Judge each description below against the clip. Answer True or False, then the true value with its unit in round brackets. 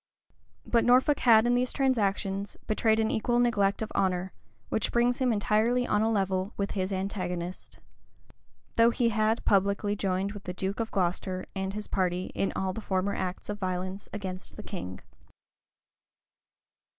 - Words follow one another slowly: False (160 wpm)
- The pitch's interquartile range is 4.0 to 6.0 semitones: False (3.0 semitones)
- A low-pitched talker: False (200 Hz)